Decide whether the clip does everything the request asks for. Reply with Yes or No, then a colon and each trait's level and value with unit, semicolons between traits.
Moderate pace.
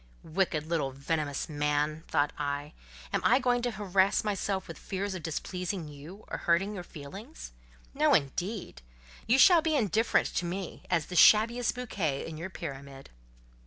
Yes: average, 160 wpm